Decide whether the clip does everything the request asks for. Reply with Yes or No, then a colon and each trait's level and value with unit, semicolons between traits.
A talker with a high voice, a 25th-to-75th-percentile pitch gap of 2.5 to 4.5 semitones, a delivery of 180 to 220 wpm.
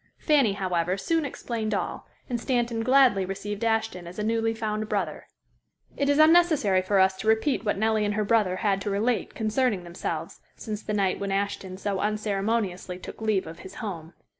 Yes: high, 210 Hz; average, 2.9 semitones; average, 185 wpm